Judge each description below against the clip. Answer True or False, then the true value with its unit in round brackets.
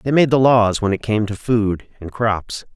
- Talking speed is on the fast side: True (240 wpm)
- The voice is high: False (110 Hz)